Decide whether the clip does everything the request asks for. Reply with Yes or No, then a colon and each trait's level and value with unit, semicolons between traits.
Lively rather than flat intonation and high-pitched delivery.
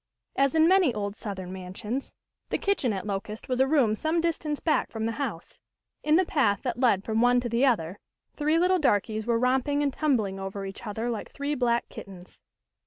Yes: wide, 5.9 semitones; high, 240 Hz